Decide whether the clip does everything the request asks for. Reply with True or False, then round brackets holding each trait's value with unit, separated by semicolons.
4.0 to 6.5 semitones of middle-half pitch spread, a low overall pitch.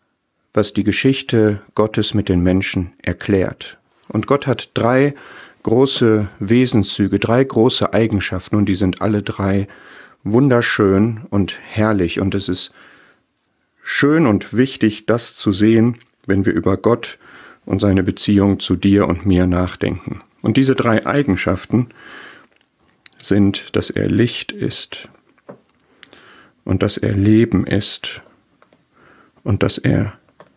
False (2.8 semitones; 105 Hz)